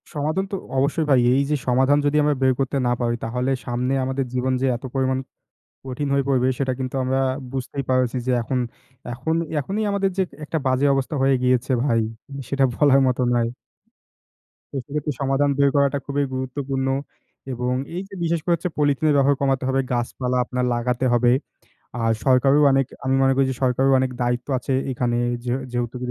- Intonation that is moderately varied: No, narrow, 2.0 semitones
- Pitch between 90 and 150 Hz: Yes, low, 135 Hz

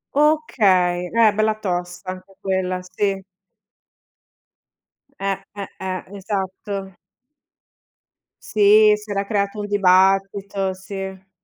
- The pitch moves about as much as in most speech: No, narrow, 1.7 semitones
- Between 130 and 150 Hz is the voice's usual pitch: No, high, 195 Hz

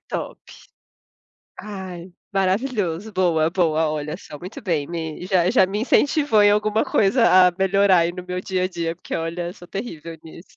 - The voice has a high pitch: No, medium, 180 Hz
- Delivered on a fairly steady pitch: No, average, 3.0 semitones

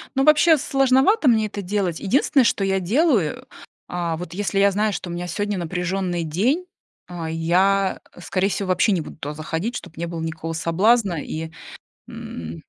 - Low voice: No, medium, 185 Hz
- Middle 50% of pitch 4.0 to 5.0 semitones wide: Yes, average, 4.4 semitones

